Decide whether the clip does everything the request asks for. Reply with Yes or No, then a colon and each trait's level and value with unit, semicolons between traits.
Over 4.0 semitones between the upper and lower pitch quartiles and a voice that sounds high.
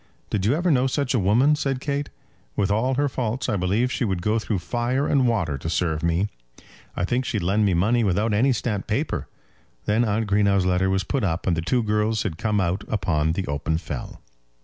No: average, 5.1 semitones; low, 105 Hz